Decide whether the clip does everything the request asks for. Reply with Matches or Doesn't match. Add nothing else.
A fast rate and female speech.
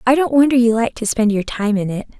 Matches